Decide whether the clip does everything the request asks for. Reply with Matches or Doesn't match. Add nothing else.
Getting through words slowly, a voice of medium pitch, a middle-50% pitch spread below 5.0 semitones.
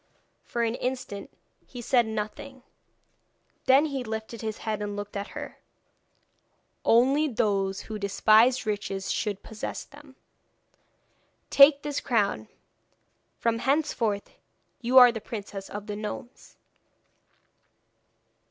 Doesn't match